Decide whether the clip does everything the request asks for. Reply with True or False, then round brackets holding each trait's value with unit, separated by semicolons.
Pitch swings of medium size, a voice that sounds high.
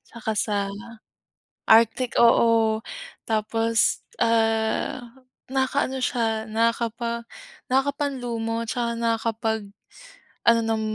False (1.3 semitones; 230 Hz)